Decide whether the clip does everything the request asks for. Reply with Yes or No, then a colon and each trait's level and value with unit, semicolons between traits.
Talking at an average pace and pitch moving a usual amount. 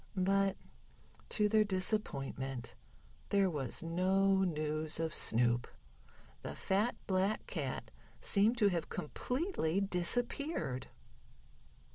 No: slow, 95 wpm; average, 4.9 semitones